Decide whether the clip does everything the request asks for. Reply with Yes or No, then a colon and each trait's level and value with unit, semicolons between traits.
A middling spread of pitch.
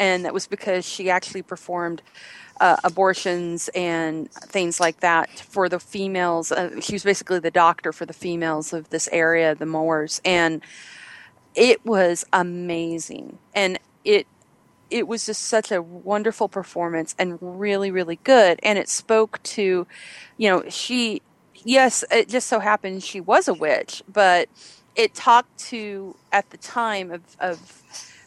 Yes: average, 3.5 semitones